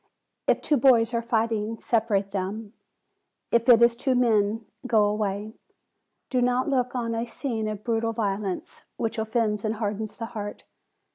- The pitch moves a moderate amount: No, narrow, 2.0 semitones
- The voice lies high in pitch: Yes, high, 225 Hz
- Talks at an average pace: Yes, average, 155 wpm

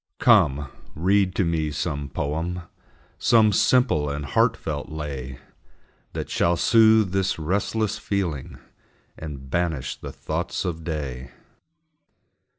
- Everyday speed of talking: No, slow, 110 wpm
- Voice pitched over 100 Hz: No, very low, 80 Hz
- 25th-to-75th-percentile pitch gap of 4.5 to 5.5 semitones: Yes, average, 5.1 semitones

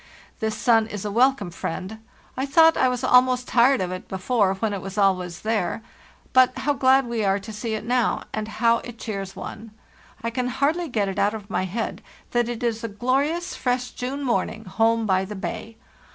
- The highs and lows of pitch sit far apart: No, average, 3.7 semitones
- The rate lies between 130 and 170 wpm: No, fast, 205 wpm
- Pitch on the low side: No, high, 230 Hz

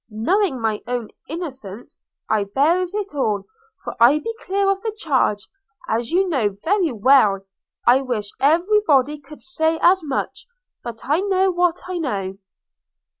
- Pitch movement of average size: No, wide, 7.8 semitones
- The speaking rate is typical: Yes, average, 155 wpm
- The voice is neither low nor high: No, very high, 285 Hz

